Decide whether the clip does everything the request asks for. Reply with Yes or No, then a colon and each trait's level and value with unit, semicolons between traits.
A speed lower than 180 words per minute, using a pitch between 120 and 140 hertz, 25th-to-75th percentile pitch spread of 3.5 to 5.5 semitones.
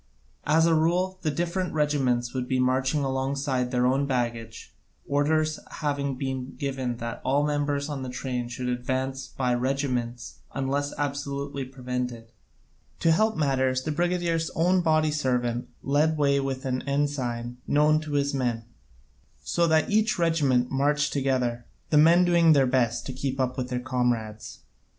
No: average, 155 wpm; low, 135 Hz; average, 3.1 semitones